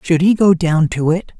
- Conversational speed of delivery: No, fast, 255 wpm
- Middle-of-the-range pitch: Yes, medium, 170 Hz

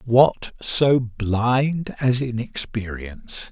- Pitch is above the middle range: No, low, 120 Hz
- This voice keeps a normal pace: No, slow, 85 wpm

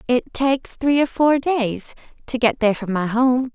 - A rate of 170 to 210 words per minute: Yes, fast, 205 wpm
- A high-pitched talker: Yes, very high, 250 Hz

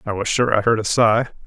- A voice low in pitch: Yes, low, 110 Hz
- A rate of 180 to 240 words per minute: No, fast, 285 wpm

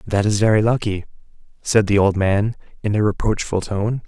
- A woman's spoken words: No, male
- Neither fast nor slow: Yes, average, 175 wpm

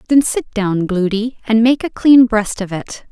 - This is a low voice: No, high, 225 Hz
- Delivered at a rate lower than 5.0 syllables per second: Yes, 4.3 syllables/s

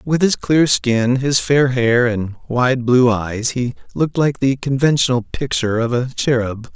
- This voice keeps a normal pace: Yes, average, 180 wpm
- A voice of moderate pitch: No, low, 125 Hz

